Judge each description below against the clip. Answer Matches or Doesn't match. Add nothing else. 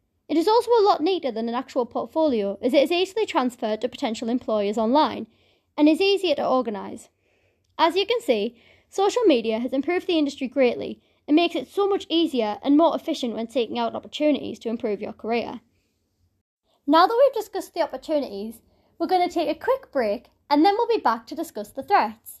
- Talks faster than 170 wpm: Matches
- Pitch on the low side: Doesn't match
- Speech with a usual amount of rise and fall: Doesn't match